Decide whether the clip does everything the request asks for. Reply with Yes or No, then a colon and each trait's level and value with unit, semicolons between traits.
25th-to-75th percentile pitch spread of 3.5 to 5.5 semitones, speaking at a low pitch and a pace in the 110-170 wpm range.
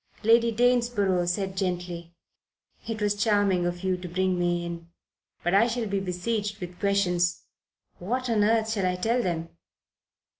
No: average, 3.8 semitones; high, 195 Hz; average, 155 wpm